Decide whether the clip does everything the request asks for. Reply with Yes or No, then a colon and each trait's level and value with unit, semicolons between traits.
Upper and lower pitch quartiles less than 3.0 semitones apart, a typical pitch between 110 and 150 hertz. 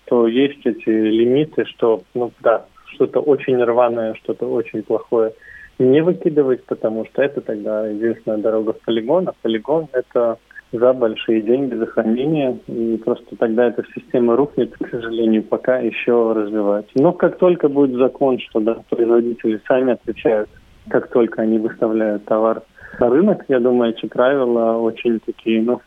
Yes: narrow, 2.4 semitones; low, 115 Hz